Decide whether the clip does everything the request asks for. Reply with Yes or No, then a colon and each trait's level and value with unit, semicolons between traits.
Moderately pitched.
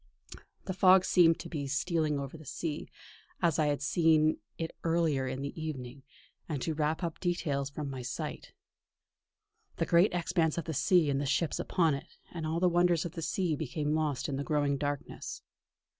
Yes: medium, 155 Hz